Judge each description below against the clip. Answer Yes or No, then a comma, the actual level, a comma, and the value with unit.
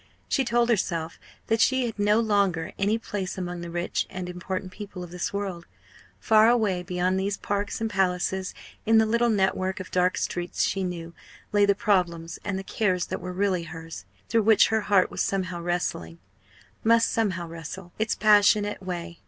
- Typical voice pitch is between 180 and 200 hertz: Yes, high, 190 Hz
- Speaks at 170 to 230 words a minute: Yes, average, 180 wpm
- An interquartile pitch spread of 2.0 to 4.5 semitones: Yes, average, 2.9 semitones